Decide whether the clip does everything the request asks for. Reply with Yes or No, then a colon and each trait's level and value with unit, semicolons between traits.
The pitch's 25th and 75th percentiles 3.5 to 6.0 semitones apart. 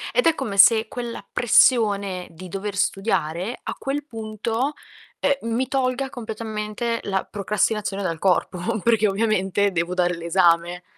Yes: average, 3.9 semitones